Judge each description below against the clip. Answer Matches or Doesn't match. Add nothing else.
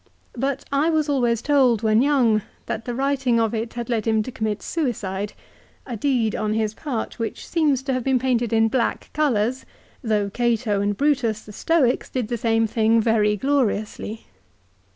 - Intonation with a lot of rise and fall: Doesn't match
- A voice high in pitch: Matches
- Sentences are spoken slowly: Doesn't match